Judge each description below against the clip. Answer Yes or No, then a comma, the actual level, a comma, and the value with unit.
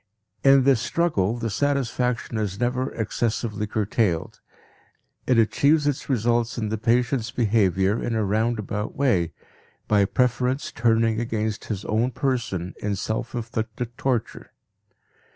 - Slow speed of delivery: Yes, slow, 125 wpm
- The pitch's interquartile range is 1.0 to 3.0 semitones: Yes, average, 2.7 semitones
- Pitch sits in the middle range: No, low, 115 Hz